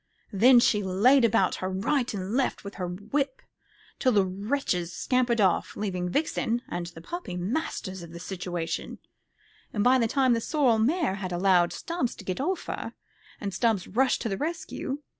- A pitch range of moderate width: No, wide, 5.8 semitones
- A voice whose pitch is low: No, high, 210 Hz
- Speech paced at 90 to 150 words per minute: No, average, 180 wpm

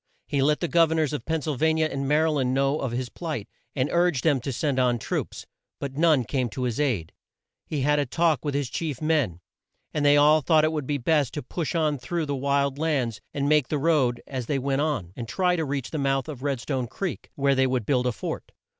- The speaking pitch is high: No, medium, 140 Hz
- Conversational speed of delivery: No, fast, 250 wpm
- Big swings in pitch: No, average, 3.2 semitones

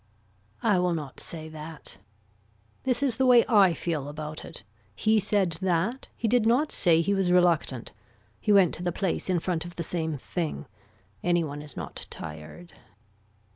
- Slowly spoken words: No, average, 175 wpm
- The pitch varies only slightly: No, average, 4.2 semitones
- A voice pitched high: No, medium, 175 Hz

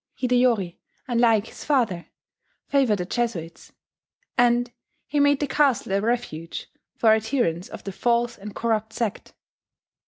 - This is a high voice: Yes, high, 230 Hz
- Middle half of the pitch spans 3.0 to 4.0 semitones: Yes, average, 3.6 semitones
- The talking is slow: Yes, slow, 130 wpm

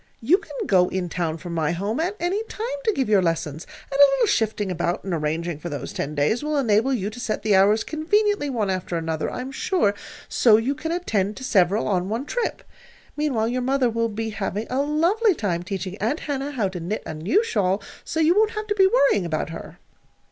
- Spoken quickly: Yes, fast, 225 wpm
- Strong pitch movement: Yes, wide, 7.9 semitones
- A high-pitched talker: Yes, high, 220 Hz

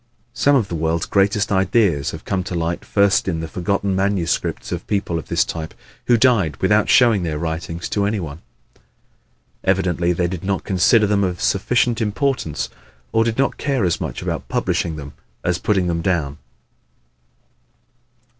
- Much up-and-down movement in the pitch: No, average, 3.8 semitones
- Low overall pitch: Yes, very low, 95 Hz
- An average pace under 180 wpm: Yes, average, 170 wpm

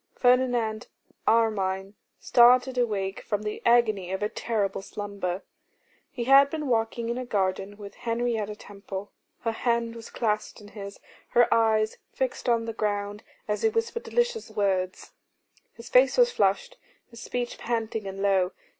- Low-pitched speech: No, high, 225 Hz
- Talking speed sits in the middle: Yes, average, 150 wpm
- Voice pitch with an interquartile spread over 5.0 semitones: No, average, 3.1 semitones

